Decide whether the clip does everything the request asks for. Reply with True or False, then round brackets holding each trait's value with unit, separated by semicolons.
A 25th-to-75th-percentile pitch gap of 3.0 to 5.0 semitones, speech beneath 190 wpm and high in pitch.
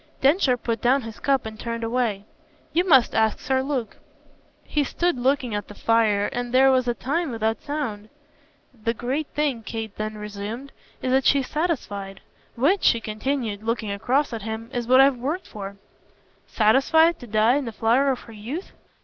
True (3.8 semitones; 180 wpm; 245 Hz)